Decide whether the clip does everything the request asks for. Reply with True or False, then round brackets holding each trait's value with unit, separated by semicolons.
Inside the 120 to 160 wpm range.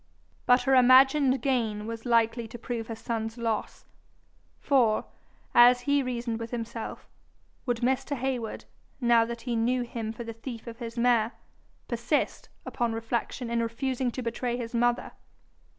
True (150 wpm)